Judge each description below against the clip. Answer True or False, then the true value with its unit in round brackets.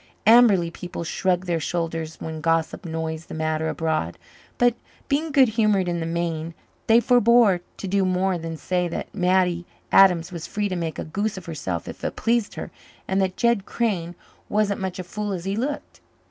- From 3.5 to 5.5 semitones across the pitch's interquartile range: True (3.9 semitones)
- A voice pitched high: False (180 Hz)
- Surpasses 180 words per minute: True (190 wpm)